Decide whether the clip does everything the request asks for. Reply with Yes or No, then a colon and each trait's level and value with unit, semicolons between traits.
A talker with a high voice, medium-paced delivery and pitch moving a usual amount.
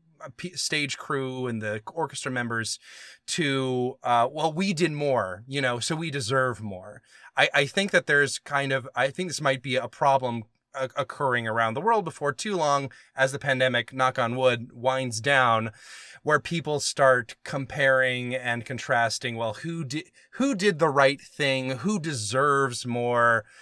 No: low, 135 Hz; average, 165 wpm; average, 3.5 semitones